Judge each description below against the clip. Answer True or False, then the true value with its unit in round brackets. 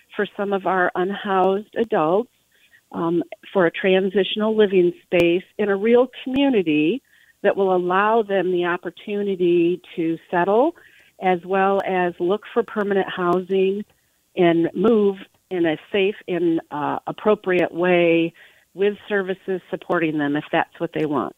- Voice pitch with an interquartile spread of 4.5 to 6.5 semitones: False (2.8 semitones)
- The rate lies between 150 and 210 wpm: False (140 wpm)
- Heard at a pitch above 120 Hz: True (190 Hz)